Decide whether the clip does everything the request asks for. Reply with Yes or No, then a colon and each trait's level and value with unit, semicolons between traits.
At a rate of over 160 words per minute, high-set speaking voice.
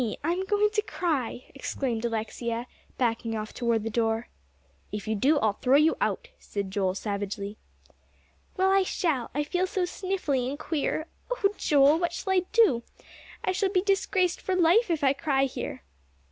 Yes: average, 170 wpm; very high, 285 Hz